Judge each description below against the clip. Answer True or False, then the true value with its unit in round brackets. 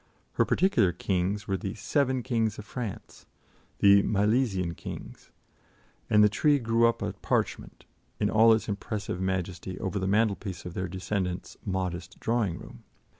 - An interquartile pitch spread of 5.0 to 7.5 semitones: False (3.4 semitones)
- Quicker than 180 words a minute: False (150 wpm)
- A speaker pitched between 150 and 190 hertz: False (100 Hz)